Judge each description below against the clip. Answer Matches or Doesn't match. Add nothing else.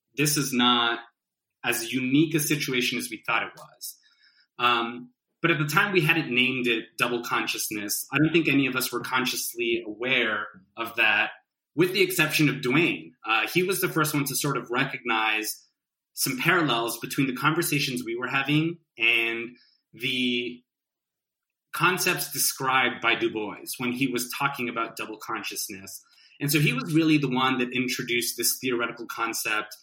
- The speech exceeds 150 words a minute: Matches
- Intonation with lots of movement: Doesn't match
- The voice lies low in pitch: Matches